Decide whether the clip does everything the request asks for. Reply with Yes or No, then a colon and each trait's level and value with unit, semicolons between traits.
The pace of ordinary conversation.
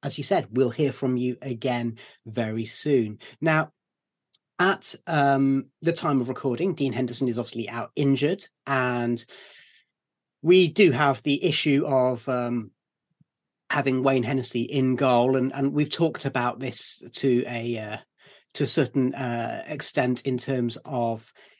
Yes: average, 145 wpm